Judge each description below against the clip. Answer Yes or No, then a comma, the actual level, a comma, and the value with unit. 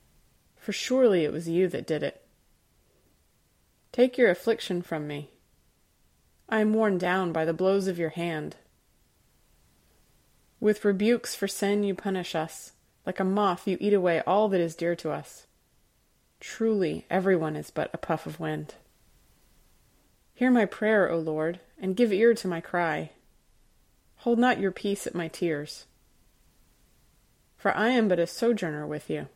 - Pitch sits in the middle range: Yes, medium, 180 Hz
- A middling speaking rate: Yes, average, 155 wpm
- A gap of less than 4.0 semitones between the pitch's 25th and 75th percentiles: No, average, 4.9 semitones